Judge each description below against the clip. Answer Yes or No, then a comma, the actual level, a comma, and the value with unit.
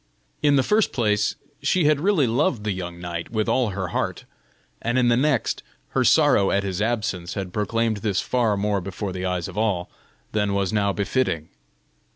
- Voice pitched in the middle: No, low, 105 Hz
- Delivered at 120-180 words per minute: No, average, 190 wpm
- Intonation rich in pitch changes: No, average, 4.0 semitones